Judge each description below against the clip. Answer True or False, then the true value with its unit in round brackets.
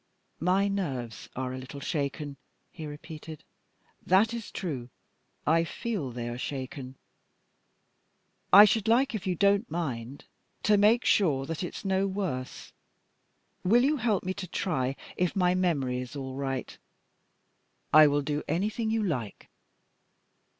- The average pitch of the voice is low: False (165 Hz)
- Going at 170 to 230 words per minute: False (140 wpm)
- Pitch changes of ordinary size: False (6.8 semitones)